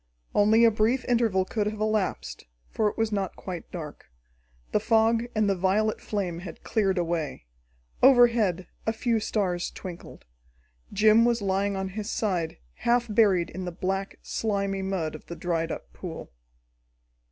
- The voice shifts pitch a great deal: No, average, 3.3 semitones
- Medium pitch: No, high, 200 Hz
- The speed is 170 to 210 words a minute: No, average, 155 wpm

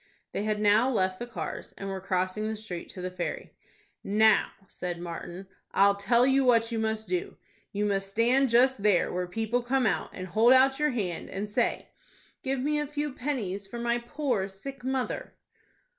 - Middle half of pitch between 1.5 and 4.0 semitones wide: No, average, 4.8 semitones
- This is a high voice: Yes, high, 220 Hz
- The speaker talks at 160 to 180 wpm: No, average, 190 wpm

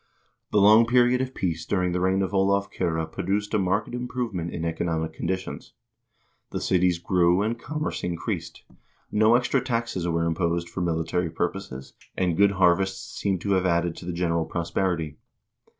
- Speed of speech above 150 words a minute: Yes, average, 165 wpm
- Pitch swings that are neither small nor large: Yes, average, 3.3 semitones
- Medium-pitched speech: No, very low, 90 Hz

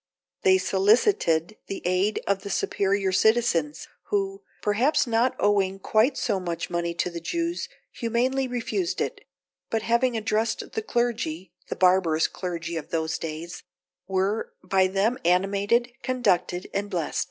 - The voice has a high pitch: Yes, high, 200 Hz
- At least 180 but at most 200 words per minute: No, average, 140 wpm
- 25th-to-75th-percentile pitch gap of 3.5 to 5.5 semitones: Yes, average, 4.6 semitones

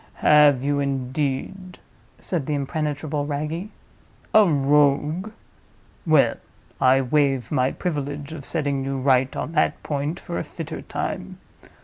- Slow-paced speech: Yes, slow, 125 wpm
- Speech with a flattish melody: Yes, narrow, 2.3 semitones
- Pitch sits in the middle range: Yes, medium, 145 Hz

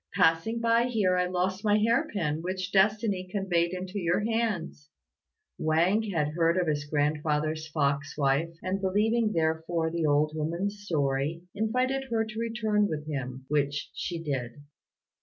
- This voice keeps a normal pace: Yes, average, 150 wpm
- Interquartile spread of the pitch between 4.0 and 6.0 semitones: Yes, average, 5.3 semitones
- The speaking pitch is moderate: Yes, medium, 175 Hz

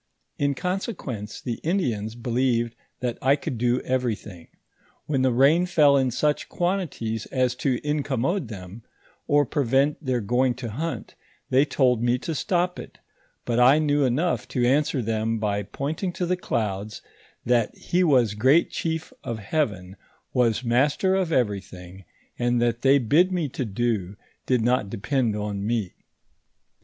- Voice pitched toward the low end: Yes, low, 125 Hz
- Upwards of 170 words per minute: No, average, 150 wpm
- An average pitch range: Yes, average, 4.6 semitones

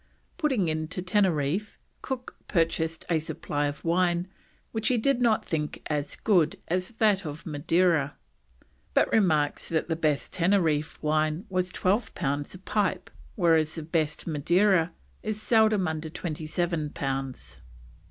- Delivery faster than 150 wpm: No, average, 140 wpm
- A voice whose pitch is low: No, medium, 170 Hz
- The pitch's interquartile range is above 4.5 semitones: No, average, 3.9 semitones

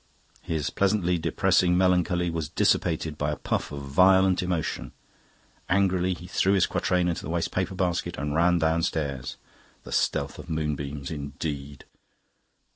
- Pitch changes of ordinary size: Yes, average, 3.5 semitones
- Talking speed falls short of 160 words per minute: Yes, average, 140 wpm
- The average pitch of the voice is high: No, very low, 85 Hz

